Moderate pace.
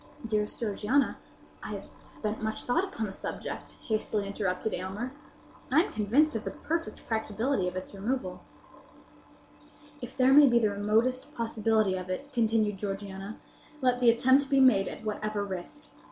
Yes: average, 155 wpm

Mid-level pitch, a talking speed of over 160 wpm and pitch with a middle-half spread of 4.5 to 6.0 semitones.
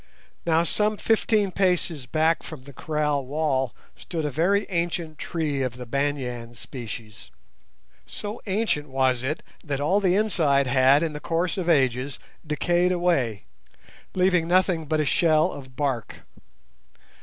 No: medium, 155 Hz; average, 145 wpm; average, 4.8 semitones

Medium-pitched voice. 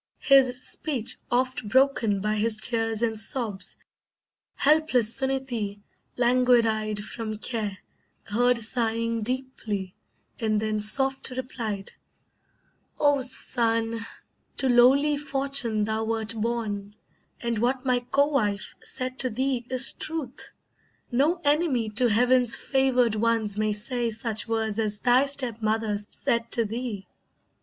No: high, 235 Hz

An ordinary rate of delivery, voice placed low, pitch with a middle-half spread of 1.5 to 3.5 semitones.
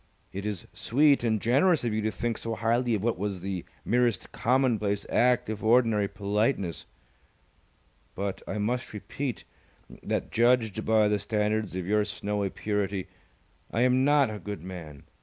Yes: average, 160 wpm; low, 110 Hz; average, 3.0 semitones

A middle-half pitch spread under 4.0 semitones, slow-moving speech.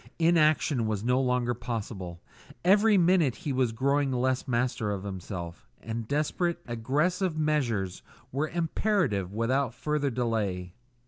No: wide, 5.4 semitones; slow, 125 wpm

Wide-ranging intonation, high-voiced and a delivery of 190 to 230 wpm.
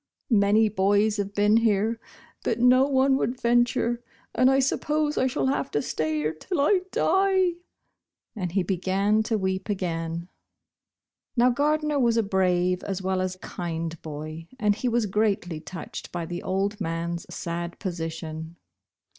No: wide, 5.7 semitones; high, 200 Hz; average, 155 wpm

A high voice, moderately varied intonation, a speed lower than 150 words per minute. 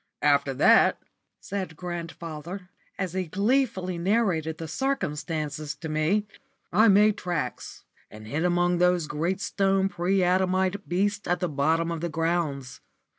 No: medium, 175 Hz; average, 3.4 semitones; slow, 135 wpm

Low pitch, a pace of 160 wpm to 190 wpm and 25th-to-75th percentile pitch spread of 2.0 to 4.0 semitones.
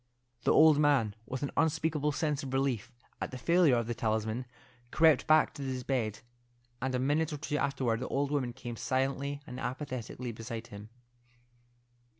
Yes: low, 130 Hz; average, 170 wpm; average, 3.6 semitones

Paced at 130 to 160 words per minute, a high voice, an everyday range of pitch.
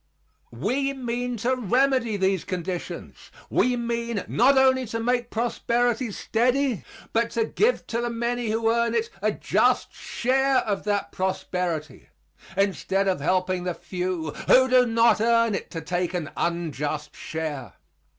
Yes: average, 145 wpm; high, 225 Hz; average, 4.9 semitones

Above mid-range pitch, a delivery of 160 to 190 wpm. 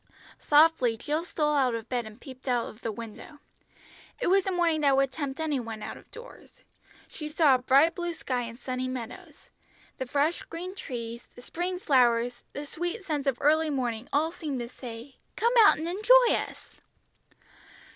Yes: very high, 280 Hz; average, 185 wpm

